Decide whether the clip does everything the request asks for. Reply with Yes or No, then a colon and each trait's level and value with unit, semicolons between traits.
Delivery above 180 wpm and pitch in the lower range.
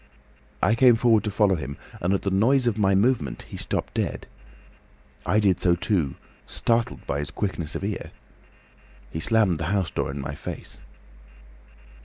No: average, 170 wpm; very low, 95 Hz